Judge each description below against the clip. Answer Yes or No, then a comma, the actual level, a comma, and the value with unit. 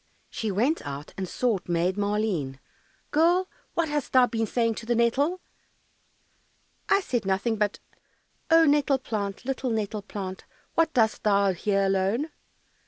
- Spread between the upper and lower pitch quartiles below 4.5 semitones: No, average, 5.3 semitones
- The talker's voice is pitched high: Yes, high, 220 Hz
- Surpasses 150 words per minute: No, average, 145 wpm